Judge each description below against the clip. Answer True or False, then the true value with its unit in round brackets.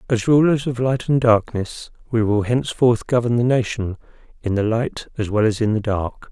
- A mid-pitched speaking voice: False (115 Hz)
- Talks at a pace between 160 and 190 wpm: False (200 wpm)